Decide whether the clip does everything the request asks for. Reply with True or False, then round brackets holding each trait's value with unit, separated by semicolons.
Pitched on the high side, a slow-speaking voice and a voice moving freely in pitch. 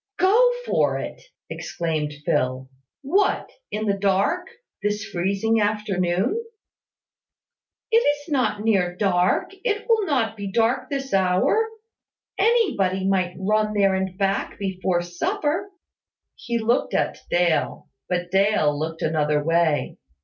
True (200 Hz; 120 wpm; 6.8 semitones)